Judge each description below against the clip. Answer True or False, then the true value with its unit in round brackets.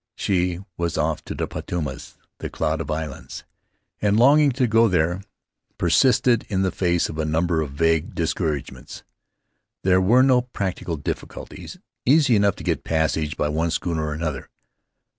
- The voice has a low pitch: True (85 Hz)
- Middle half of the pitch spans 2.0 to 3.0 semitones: False (4.7 semitones)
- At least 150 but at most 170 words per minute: True (160 wpm)